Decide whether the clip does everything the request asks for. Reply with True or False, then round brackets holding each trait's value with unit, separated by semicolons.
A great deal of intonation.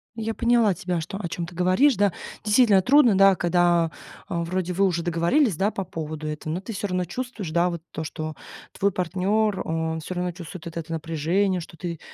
False (3.3 semitones)